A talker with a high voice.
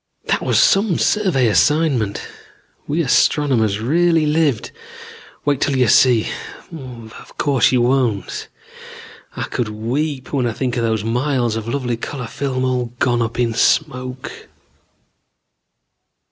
No: low, 130 Hz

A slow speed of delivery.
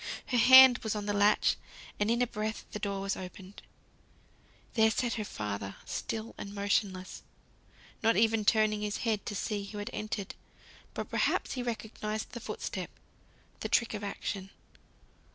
No: average, 165 wpm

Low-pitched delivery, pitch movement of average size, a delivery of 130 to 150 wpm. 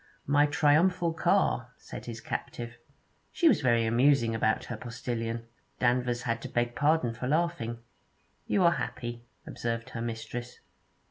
Yes: low, 120 Hz; average, 3.8 semitones; average, 140 wpm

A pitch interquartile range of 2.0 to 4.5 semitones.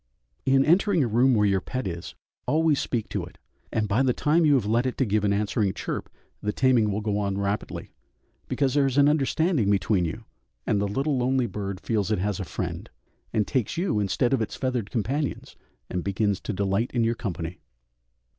No: average, 4.9 semitones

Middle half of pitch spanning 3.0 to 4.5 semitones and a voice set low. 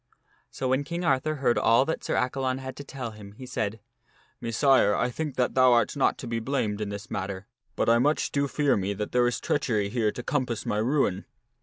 Yes: average, 4.0 semitones; low, 125 Hz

